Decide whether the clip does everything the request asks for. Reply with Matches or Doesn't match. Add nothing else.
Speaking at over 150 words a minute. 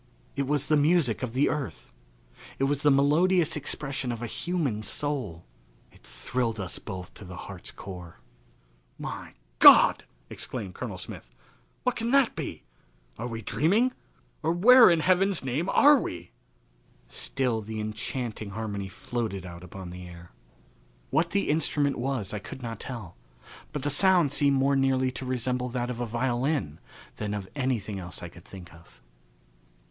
Matches